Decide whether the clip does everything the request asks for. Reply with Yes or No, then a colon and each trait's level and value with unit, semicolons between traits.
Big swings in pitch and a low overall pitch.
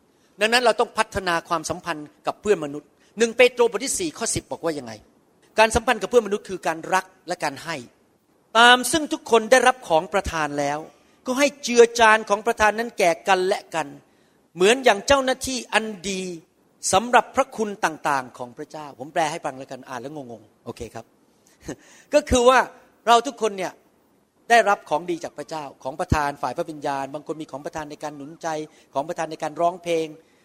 No: wide, 7.5 semitones; medium, 180 Hz